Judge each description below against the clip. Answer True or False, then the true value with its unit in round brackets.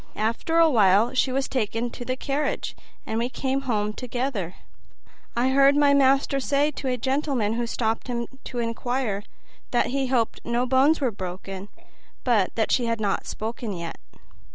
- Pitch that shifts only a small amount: False (3.4 semitones)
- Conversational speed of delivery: True (165 wpm)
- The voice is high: True (245 Hz)